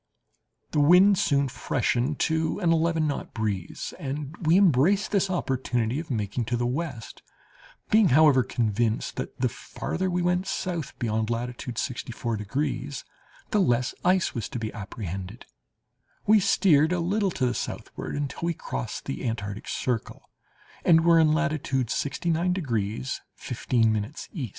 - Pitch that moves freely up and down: Yes, wide, 6.3 semitones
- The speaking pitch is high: No, medium, 140 Hz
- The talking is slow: No, average, 150 wpm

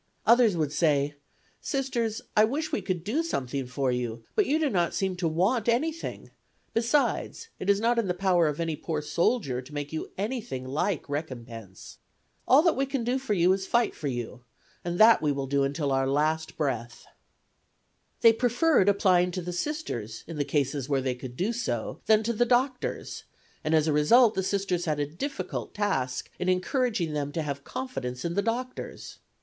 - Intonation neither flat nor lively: No, wide, 8.6 semitones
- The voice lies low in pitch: No, medium, 175 Hz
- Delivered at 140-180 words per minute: No, average, 190 wpm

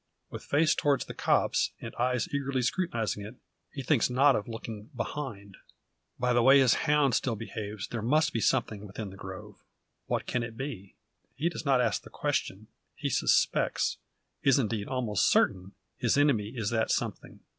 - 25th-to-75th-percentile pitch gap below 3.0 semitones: No, average, 4.4 semitones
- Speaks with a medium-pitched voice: No, low, 120 Hz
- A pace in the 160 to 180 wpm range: Yes, average, 175 wpm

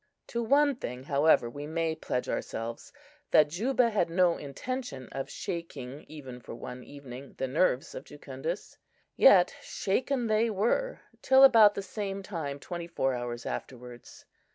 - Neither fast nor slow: Yes, average, 150 wpm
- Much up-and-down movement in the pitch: Yes, wide, 7.9 semitones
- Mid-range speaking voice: Yes, medium, 160 Hz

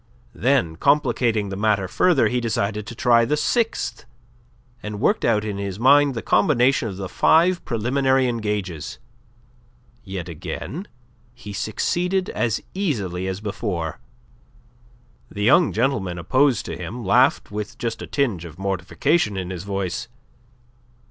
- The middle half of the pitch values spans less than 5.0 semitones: No, wide, 5.5 semitones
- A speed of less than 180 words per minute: Yes, slow, 135 wpm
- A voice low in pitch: Yes, low, 110 Hz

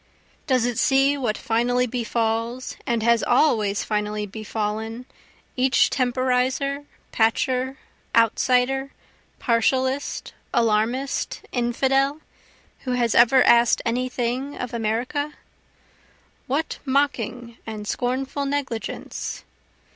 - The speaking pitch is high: Yes, high, 245 Hz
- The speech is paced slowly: Yes, slow, 95 wpm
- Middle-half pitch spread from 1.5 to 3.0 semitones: Yes, average, 2.7 semitones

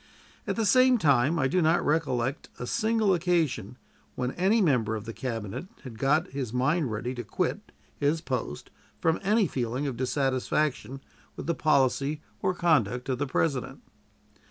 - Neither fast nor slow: Yes, average, 160 wpm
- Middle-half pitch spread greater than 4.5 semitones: Yes, average, 5.1 semitones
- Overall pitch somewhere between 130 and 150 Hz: Yes, medium, 140 Hz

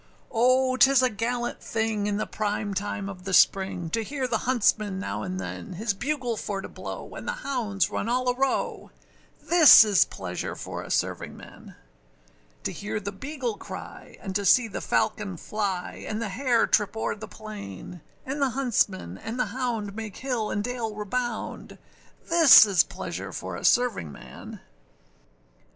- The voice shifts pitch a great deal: No, average, 3.9 semitones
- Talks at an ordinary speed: Yes, average, 170 wpm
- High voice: Yes, high, 220 Hz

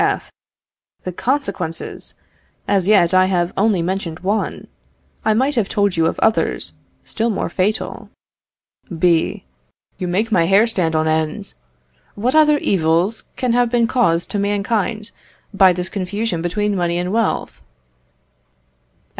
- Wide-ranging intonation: No, average, 4.0 semitones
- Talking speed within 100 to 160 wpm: Yes, average, 140 wpm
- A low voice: No, high, 195 Hz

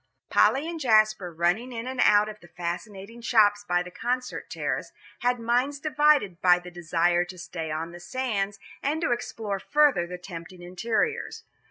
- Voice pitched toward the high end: Yes, high, 205 Hz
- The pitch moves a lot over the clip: Yes, wide, 5.8 semitones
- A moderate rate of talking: Yes, average, 170 wpm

